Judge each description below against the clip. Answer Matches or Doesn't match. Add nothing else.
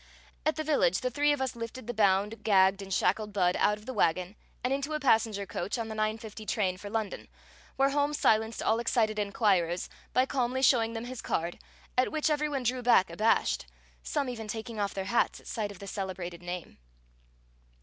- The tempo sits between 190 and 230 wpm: Matches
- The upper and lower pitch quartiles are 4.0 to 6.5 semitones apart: Matches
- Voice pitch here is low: Doesn't match